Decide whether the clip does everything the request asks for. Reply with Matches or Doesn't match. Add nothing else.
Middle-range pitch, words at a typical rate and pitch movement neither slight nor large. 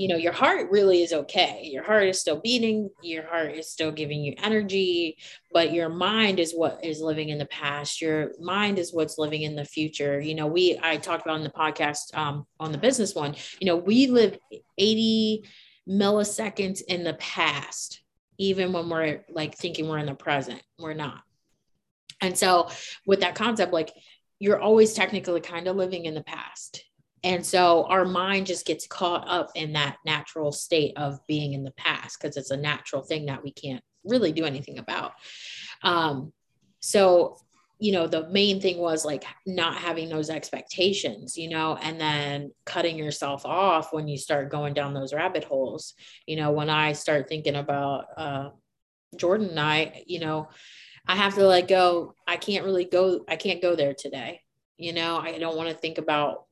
Matches